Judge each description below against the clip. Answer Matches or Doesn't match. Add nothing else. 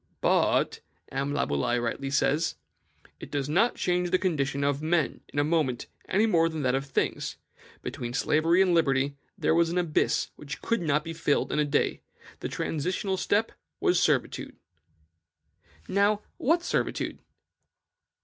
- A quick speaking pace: Doesn't match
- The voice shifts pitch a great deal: Doesn't match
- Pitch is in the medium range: Matches